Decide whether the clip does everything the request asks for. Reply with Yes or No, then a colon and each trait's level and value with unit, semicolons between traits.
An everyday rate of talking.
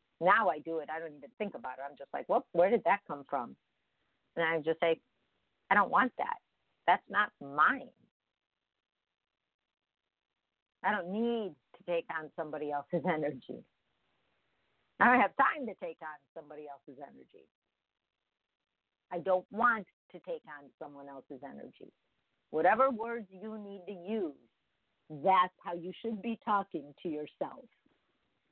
Yes: average, 150 wpm